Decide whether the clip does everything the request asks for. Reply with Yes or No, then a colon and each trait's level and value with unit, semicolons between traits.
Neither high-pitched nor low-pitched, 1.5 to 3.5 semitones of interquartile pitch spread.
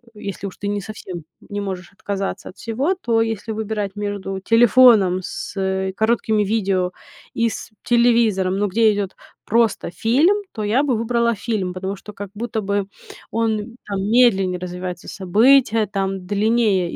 No: high, 205 Hz; average, 3.0 semitones